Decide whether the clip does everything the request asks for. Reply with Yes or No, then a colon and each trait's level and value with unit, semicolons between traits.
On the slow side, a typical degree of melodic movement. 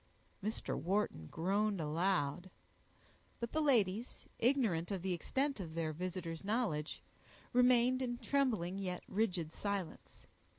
No: slow, 120 wpm; wide, 5.8 semitones